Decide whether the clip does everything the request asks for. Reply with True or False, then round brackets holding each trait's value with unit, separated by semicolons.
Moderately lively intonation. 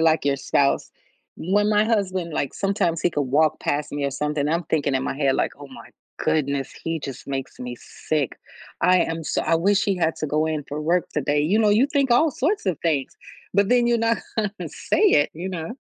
False (5.7 semitones)